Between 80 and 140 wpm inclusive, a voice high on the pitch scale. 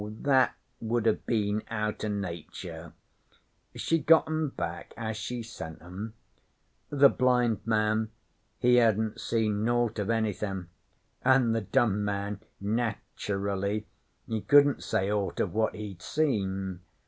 No: slow, 135 wpm; low, 110 Hz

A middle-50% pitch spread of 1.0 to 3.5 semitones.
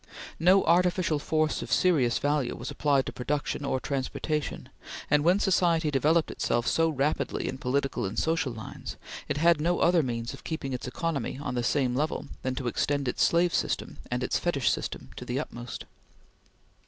No: average, 4.2 semitones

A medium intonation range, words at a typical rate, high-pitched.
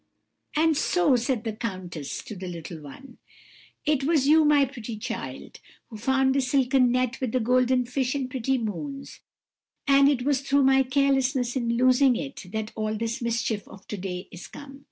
Yes: average, 3.5 semitones; average, 180 wpm; very high, 255 Hz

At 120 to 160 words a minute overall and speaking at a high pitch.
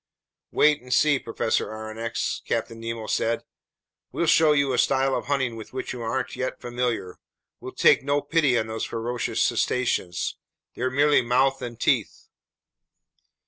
No: average, 150 wpm; low, 125 Hz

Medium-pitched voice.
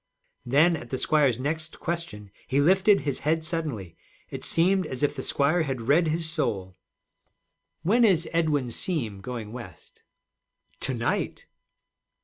Yes: medium, 150 Hz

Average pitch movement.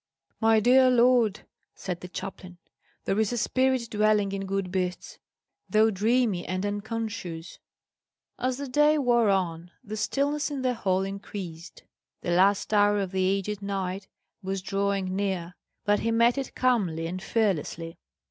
Yes: average, 3.9 semitones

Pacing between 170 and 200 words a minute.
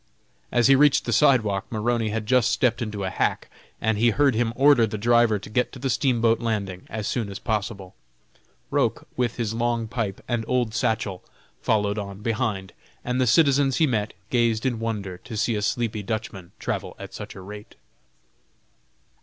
Yes: average, 180 wpm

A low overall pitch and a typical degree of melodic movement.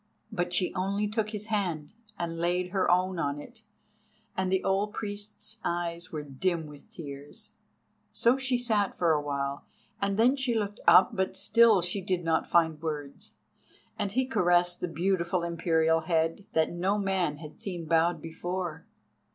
No: medium, 180 Hz; average, 3.6 semitones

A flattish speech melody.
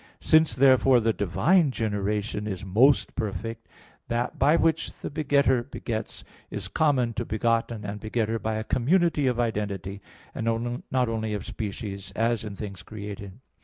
No: average, 3.7 semitones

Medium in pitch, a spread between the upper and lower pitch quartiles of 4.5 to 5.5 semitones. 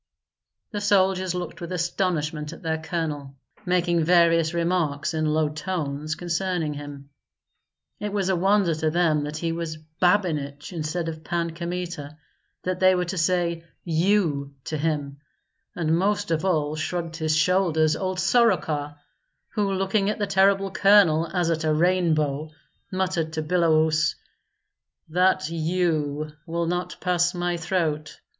No: medium, 170 Hz; average, 2.8 semitones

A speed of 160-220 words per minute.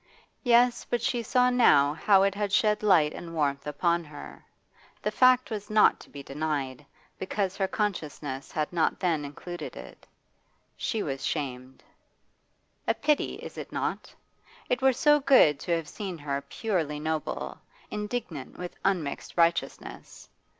No: average, 150 wpm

